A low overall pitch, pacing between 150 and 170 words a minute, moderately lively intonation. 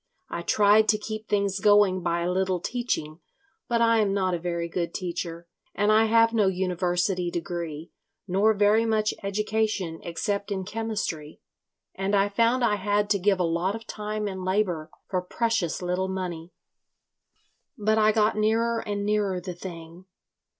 No: high, 200 Hz; average, 165 wpm; average, 3.2 semitones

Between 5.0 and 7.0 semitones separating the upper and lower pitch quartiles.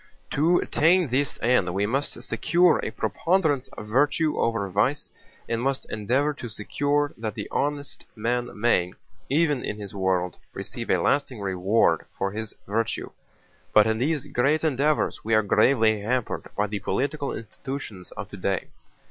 Yes: wide, 5.5 semitones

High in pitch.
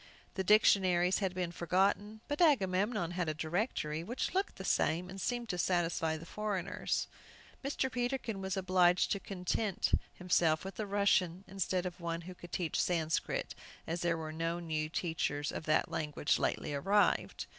No: medium, 180 Hz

